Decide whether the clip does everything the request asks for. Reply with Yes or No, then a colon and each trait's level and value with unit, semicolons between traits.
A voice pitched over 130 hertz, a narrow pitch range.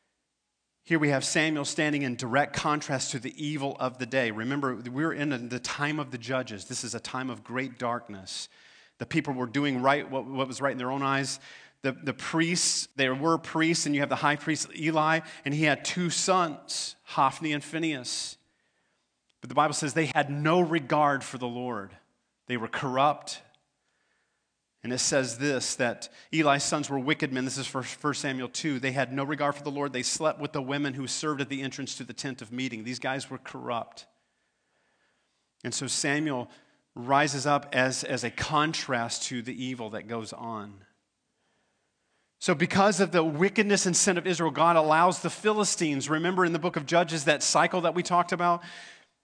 No: medium, 140 Hz; average, 3.6 semitones